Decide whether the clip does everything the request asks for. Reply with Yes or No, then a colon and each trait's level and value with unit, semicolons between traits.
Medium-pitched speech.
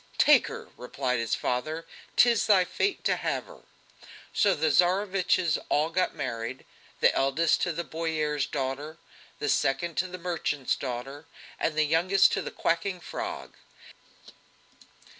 Yes: medium, 160 Hz